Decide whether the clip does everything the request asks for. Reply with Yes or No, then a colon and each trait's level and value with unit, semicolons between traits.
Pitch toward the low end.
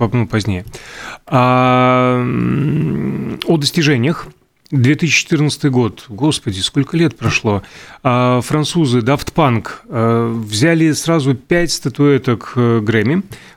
Yes: low, 125 Hz